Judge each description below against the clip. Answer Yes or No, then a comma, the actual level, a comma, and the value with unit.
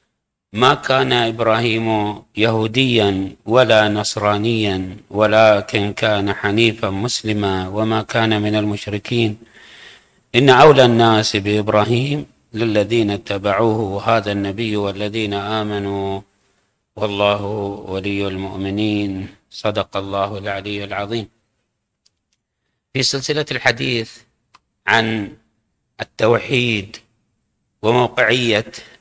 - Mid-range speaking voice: No, low, 105 Hz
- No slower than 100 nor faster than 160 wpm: No, average, 75 wpm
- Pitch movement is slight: Yes, narrow, 2.0 semitones